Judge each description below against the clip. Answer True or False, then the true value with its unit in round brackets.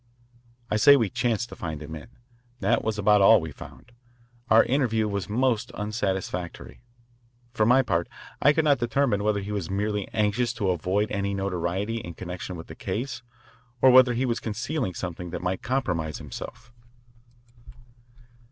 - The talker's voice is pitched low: True (105 Hz)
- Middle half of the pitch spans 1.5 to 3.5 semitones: False (4.5 semitones)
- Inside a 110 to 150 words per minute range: False (160 wpm)